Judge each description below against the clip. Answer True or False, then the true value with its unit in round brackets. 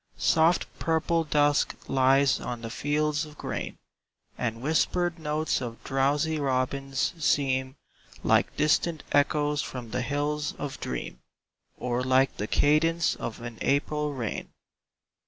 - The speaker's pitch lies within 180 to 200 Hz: False (145 Hz)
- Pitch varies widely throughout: False (2.8 semitones)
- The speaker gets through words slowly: True (125 wpm)